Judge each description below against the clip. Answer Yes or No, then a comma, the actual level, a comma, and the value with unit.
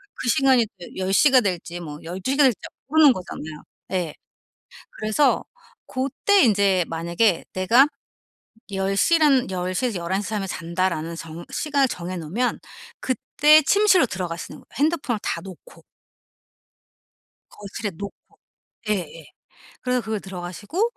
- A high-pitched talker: Yes, high, 200 Hz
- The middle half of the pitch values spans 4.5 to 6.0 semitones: No, wide, 6.8 semitones